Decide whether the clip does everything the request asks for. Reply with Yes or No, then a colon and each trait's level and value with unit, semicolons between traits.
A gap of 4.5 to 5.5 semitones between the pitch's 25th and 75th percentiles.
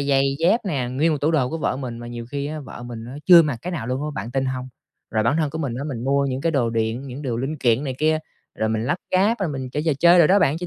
No: average, 4.1 semitones